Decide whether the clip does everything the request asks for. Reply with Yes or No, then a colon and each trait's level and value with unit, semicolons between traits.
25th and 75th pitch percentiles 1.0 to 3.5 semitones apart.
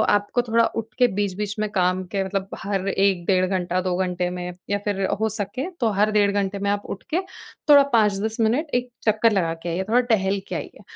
Yes: narrow, 2.5 semitones